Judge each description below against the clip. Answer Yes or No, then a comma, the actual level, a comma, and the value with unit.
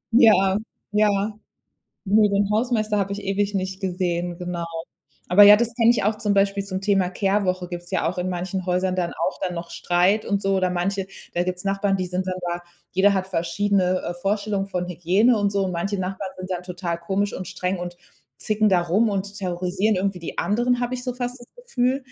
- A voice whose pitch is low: No, high, 195 Hz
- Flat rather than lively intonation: Yes, narrow, 2.3 semitones